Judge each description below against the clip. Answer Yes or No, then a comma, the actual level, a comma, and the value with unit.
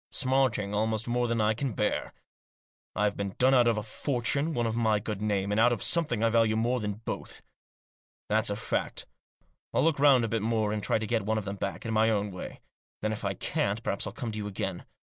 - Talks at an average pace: No, fast, 235 wpm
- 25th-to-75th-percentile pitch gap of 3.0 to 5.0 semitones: No, narrow, 2.4 semitones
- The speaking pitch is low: Yes, low, 110 Hz